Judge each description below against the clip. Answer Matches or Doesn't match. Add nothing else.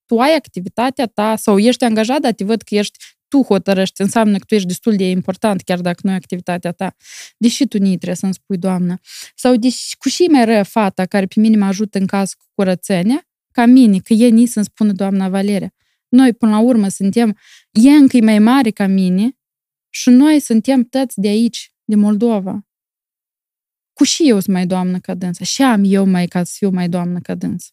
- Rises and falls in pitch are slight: Doesn't match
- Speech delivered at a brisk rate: Matches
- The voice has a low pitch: Doesn't match